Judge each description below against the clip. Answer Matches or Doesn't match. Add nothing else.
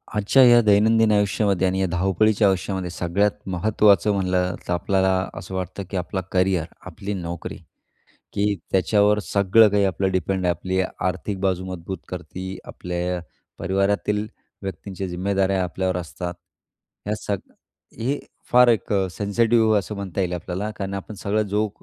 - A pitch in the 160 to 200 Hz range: Doesn't match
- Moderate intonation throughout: Doesn't match